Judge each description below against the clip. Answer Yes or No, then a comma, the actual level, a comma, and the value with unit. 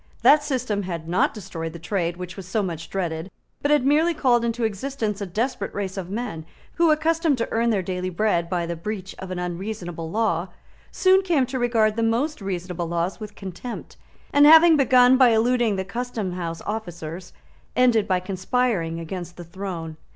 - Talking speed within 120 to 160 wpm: No, average, 185 wpm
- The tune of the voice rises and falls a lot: Yes, wide, 5.9 semitones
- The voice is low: No, high, 200 Hz